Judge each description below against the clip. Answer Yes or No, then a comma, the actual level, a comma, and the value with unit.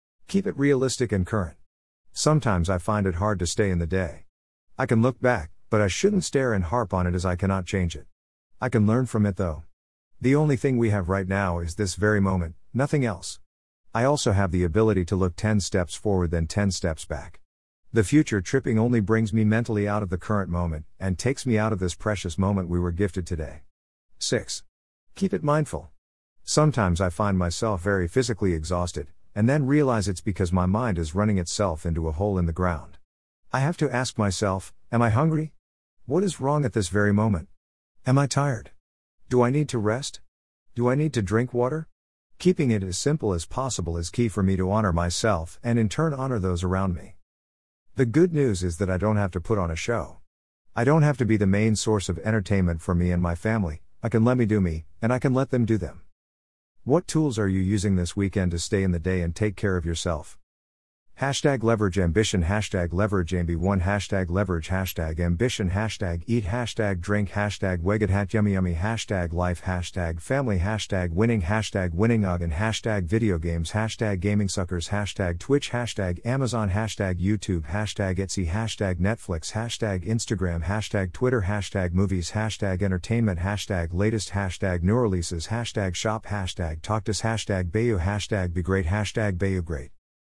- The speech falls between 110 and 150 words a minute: No, average, 195 wpm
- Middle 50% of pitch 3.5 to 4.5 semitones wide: Yes, average, 4.1 semitones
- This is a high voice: No, low, 100 Hz